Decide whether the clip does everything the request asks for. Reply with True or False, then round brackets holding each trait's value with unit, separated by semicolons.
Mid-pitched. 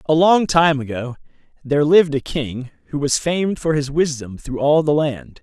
True (145 Hz)